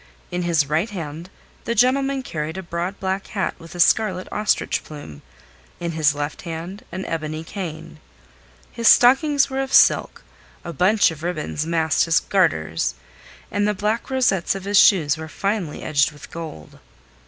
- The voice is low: No, medium, 175 Hz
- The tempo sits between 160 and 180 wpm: Yes, average, 165 wpm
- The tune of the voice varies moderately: Yes, average, 4.6 semitones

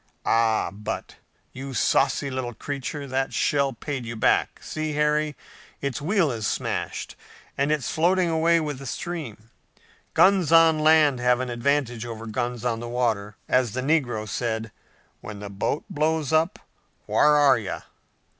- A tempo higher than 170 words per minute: No, average, 155 wpm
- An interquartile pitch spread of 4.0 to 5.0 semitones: Yes, average, 4.6 semitones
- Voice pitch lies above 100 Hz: Yes, low, 135 Hz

